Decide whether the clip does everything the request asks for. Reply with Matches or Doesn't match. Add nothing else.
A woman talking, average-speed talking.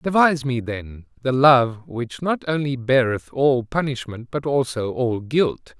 Doesn't match